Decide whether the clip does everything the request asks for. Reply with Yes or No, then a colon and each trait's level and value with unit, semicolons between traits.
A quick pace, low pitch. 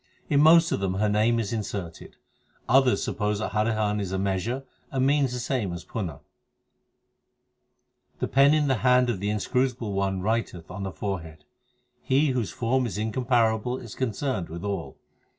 No: average, 170 wpm; low, 110 Hz